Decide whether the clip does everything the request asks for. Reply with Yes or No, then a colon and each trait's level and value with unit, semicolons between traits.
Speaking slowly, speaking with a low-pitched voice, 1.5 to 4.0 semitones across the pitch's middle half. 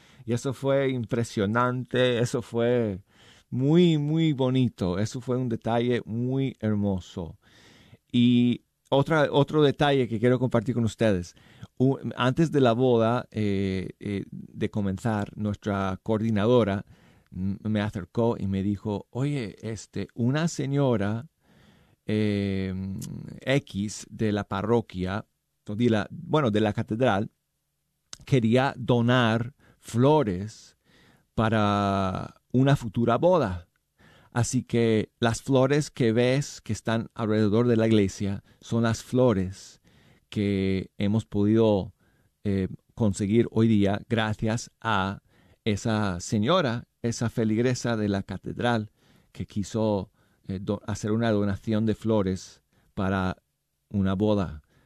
Yes: slow, 115 wpm; low, 110 Hz; average, 3.4 semitones